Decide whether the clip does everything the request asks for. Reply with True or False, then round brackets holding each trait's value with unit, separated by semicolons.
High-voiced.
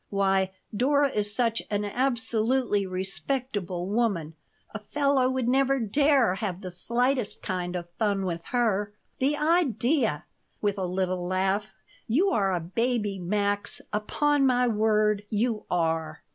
True (210 Hz)